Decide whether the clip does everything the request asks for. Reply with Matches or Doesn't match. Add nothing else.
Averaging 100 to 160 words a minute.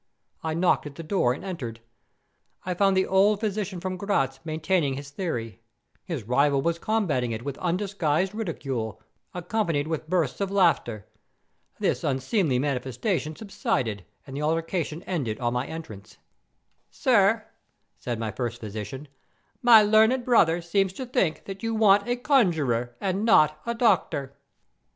Matches